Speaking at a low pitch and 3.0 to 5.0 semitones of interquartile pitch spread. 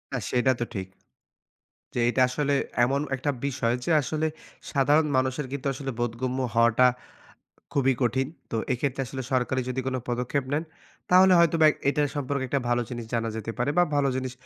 No: low, 130 Hz; narrow, 2.5 semitones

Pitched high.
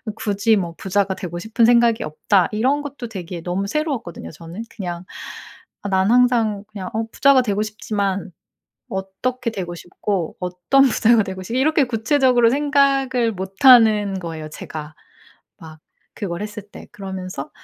Yes: high, 205 Hz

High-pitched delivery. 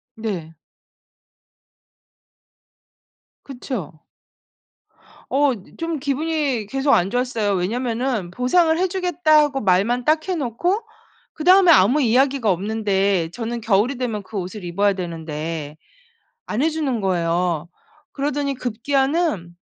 Yes: high, 240 Hz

